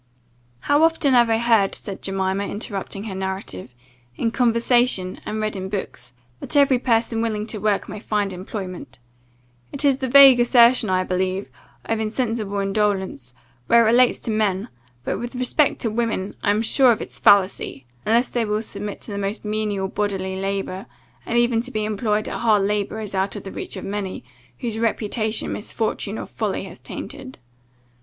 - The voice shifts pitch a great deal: No, average, 3.1 semitones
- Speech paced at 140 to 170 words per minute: No, average, 180 wpm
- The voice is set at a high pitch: Yes, high, 215 Hz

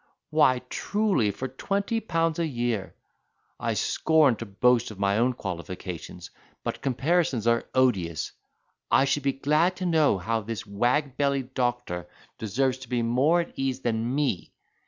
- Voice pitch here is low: Yes, low, 125 Hz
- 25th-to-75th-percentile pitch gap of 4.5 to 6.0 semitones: Yes, average, 4.8 semitones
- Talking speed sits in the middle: Yes, average, 150 wpm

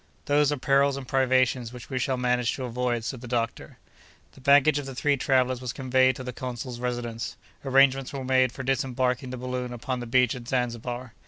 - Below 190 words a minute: No, average, 200 wpm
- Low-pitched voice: Yes, low, 130 Hz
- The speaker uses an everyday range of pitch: No, narrow, 1.5 semitones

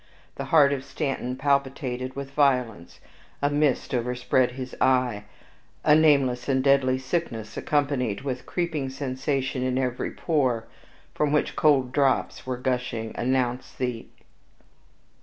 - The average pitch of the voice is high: No, low, 130 Hz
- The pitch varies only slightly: Yes, narrow, 2.0 semitones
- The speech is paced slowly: Yes, slow, 130 wpm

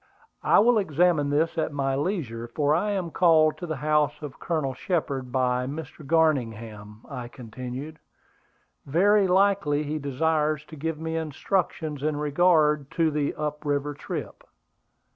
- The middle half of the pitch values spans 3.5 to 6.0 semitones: No, average, 2.9 semitones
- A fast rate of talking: No, average, 145 wpm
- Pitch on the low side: No, medium, 150 Hz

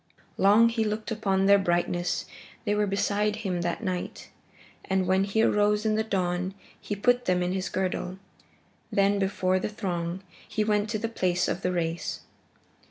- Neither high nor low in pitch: No, high, 195 Hz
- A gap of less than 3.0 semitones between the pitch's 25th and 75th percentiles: Yes, narrow, 2.5 semitones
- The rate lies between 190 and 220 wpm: No, average, 170 wpm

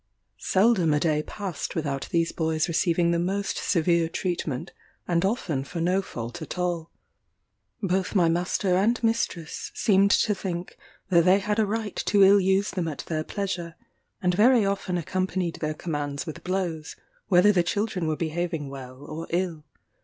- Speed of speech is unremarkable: Yes, average, 165 wpm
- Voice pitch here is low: No, medium, 175 Hz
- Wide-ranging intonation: No, average, 3.2 semitones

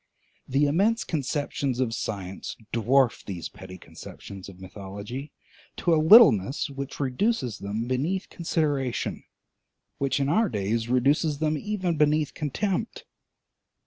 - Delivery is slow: Yes, slow, 120 wpm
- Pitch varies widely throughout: Yes, wide, 5.8 semitones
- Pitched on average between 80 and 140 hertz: Yes, low, 135 Hz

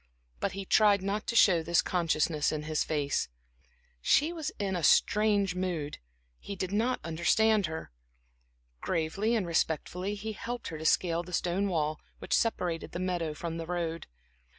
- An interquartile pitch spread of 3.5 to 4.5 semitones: Yes, average, 3.9 semitones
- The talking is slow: No, average, 165 wpm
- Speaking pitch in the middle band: Yes, medium, 180 Hz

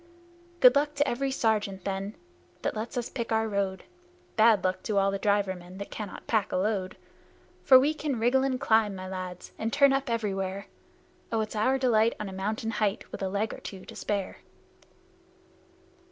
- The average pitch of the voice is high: Yes, high, 215 Hz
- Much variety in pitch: No, average, 3.6 semitones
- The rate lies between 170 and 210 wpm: Yes, average, 190 wpm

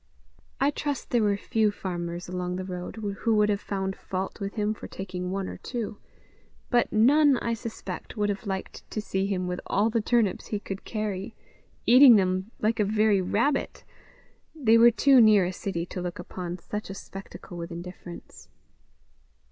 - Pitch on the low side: No, high, 205 Hz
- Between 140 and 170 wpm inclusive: No, average, 180 wpm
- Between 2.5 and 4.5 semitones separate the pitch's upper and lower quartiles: Yes, average, 3.3 semitones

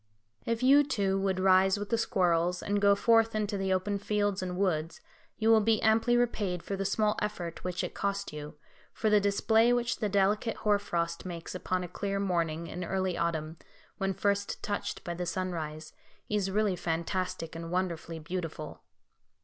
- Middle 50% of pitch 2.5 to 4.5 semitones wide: Yes, average, 3.2 semitones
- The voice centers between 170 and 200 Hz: Yes, high, 190 Hz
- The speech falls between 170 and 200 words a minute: Yes, average, 180 wpm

